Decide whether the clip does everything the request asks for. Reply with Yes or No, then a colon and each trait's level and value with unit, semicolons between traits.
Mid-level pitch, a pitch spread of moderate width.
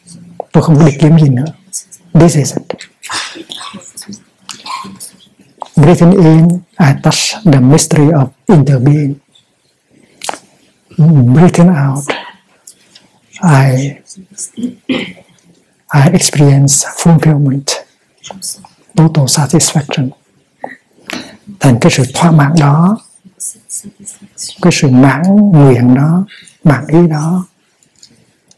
Yes: medium, 160 Hz; average, 4.0 semitones